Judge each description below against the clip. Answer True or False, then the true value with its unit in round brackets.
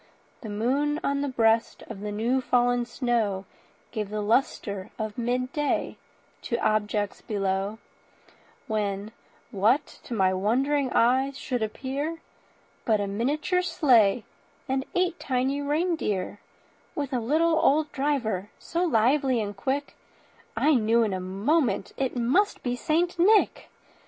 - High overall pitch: True (245 Hz)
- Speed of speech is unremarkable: False (130 wpm)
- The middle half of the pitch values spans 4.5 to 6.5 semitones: True (5.1 semitones)